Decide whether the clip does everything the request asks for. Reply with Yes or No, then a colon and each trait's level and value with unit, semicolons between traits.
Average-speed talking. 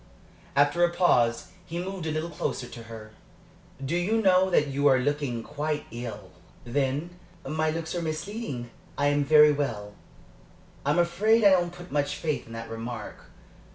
Yes: average, 170 wpm